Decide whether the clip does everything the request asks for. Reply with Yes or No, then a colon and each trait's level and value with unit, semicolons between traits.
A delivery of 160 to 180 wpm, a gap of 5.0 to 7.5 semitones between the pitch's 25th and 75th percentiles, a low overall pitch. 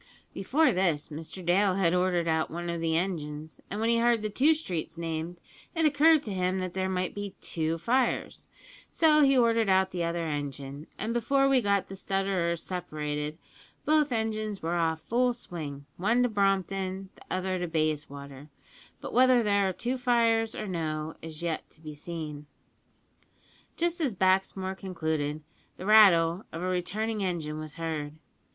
No: average, 170 wpm; average, 5.3 semitones; medium, 185 Hz